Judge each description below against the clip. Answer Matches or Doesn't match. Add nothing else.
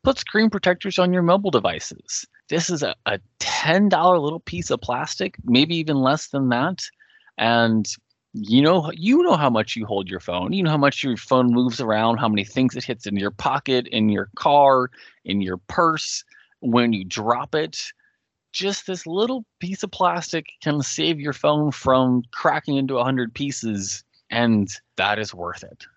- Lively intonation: Matches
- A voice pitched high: Doesn't match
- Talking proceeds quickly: Doesn't match